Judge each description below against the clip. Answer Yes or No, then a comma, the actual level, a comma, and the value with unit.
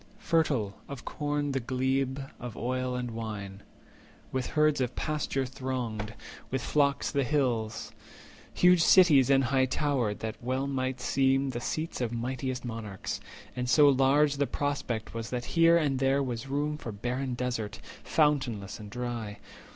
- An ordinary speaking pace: Yes, average, 155 wpm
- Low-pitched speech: Yes, low, 130 Hz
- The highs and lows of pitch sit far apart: No, average, 3.0 semitones